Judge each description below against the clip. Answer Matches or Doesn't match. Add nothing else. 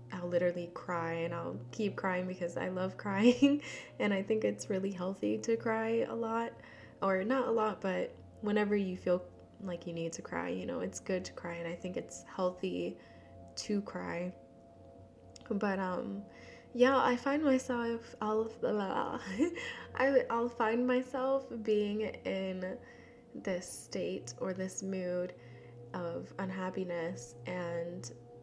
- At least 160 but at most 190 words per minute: Doesn't match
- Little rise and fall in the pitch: Doesn't match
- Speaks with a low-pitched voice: Doesn't match